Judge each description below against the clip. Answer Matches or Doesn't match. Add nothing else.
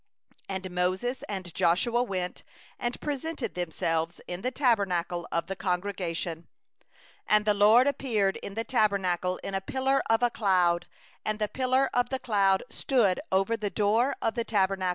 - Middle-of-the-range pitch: Doesn't match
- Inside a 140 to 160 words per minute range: Matches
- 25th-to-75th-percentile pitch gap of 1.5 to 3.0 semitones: Doesn't match